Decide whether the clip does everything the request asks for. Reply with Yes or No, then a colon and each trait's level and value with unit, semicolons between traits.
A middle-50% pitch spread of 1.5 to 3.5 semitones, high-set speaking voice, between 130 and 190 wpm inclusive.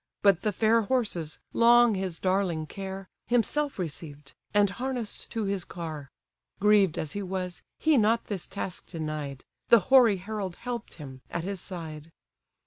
No: average, 4.9 semitones; high, 195 Hz; average, 150 wpm